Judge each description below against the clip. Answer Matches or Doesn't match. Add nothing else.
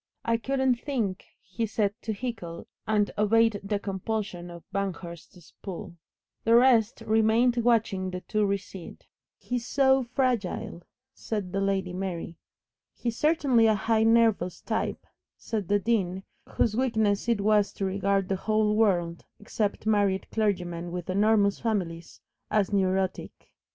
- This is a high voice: Matches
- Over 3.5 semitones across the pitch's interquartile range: Doesn't match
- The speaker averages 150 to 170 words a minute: Doesn't match